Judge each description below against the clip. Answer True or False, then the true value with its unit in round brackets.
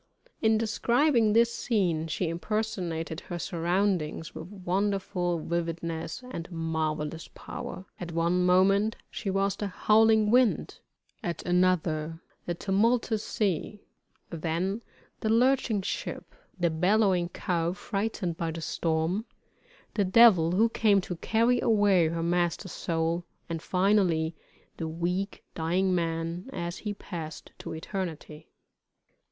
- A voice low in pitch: False (180 Hz)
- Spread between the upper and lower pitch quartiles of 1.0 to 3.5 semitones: False (3.9 semitones)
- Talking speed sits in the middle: False (120 wpm)